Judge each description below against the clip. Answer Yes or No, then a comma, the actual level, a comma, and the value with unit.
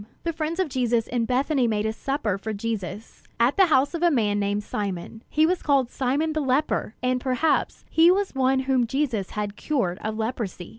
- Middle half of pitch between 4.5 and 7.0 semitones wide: Yes, wide, 5.4 semitones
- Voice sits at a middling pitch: No, very high, 250 Hz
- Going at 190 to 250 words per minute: Yes, average, 200 wpm